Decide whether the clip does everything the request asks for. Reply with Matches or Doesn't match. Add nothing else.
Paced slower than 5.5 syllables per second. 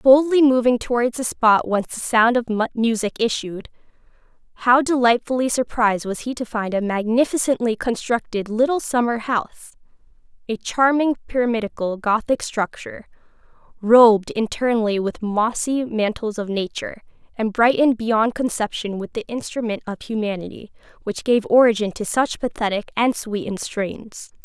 Matches